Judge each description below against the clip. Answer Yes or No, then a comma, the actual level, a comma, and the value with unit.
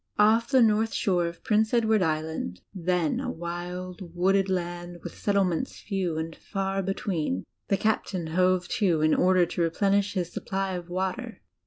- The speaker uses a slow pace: No, average, 160 wpm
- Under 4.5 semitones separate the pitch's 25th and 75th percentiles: Yes, narrow, 2.5 semitones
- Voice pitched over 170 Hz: Yes, medium, 185 Hz